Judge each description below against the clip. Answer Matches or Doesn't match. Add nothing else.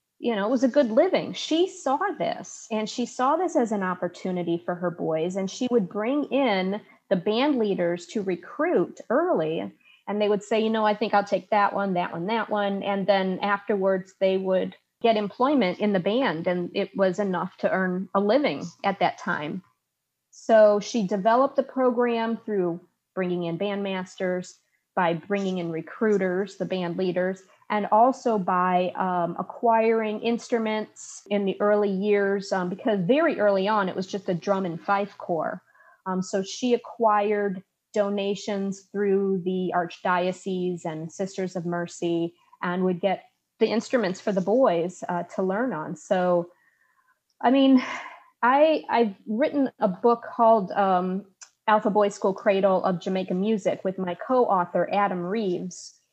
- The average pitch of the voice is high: Matches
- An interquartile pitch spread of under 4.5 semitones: Matches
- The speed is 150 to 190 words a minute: Matches